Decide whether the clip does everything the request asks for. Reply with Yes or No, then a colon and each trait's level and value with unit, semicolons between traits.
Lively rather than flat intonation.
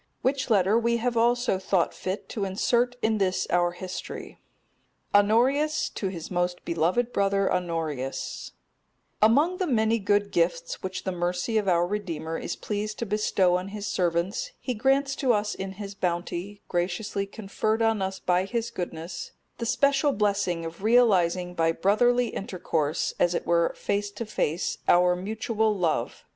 No: average, 4.1 semitones